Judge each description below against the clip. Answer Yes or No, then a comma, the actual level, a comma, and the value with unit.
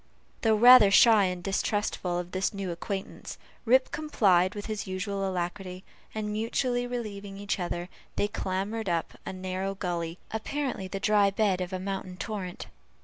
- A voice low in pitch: No, high, 195 Hz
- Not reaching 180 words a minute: Yes, average, 155 wpm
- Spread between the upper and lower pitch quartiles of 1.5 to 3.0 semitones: Yes, narrow, 2.6 semitones